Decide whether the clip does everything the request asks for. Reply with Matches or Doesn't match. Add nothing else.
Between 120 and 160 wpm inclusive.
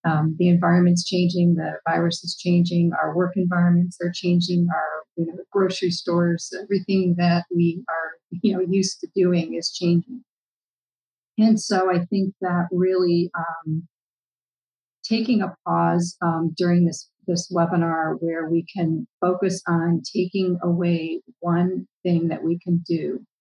Matches